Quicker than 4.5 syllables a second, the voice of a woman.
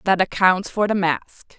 Yes: 5.3 syllables/s; female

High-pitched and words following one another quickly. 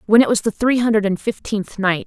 Yes: high, 210 Hz; fast, 260 wpm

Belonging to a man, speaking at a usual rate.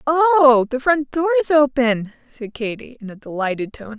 No: female; average, 180 wpm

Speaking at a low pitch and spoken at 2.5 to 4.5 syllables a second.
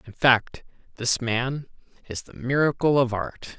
Yes: low, 125 Hz; 4.1 syllables/s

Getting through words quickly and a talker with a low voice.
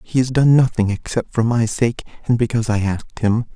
Yes: fast, 220 wpm; low, 115 Hz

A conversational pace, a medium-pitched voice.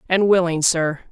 Yes: average, 160 wpm; medium, 175 Hz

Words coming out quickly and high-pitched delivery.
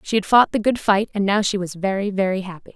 Yes: fast, 285 wpm; high, 200 Hz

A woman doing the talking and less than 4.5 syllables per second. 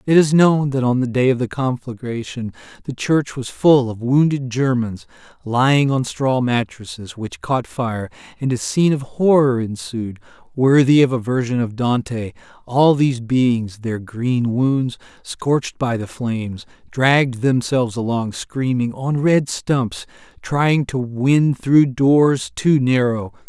No: male; 4.0 syllables/s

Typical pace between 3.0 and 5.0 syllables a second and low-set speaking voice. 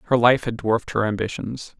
No: 5.7 syllables/s; low, 115 Hz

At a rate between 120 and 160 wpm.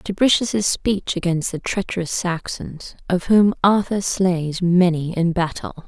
Yes: slow, 135 wpm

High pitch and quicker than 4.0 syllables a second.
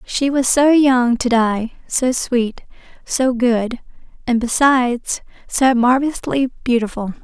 No: very high, 250 Hz; 3.9 syllables/s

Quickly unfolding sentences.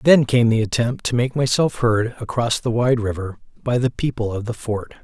Yes: fast, 215 wpm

